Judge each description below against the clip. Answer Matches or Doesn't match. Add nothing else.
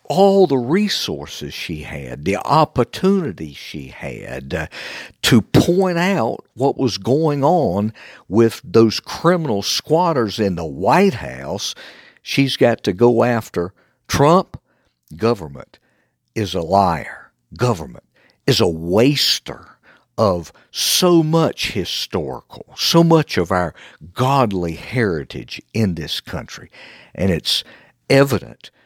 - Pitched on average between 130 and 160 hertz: Doesn't match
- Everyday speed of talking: Doesn't match